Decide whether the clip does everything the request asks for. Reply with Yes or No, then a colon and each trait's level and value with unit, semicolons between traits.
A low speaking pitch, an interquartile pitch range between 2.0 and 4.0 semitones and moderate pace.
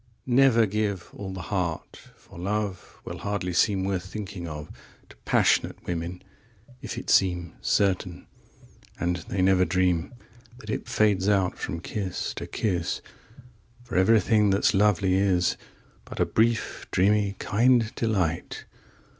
No: low, 100 Hz; average, 3.0 semitones; slow, 115 wpm